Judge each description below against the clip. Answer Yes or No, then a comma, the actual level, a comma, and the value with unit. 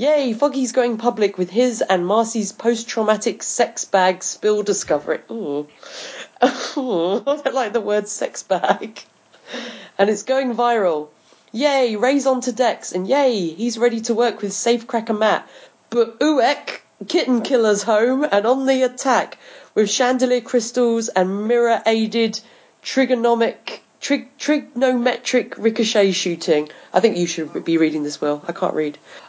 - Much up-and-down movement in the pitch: No, average, 3.8 semitones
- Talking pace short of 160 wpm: Yes, average, 140 wpm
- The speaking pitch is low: No, high, 230 Hz